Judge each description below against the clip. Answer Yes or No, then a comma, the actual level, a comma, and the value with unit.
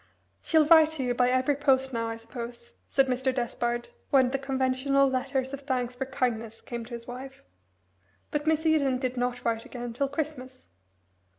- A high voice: Yes, very high, 260 Hz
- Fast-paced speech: No, average, 180 wpm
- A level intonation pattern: Yes, narrow, 2.1 semitones